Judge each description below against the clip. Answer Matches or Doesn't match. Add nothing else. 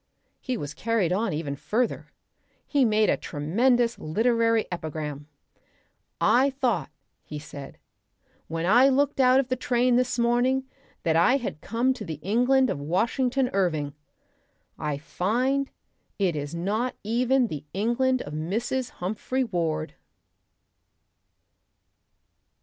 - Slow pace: Matches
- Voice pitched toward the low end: Doesn't match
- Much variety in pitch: Matches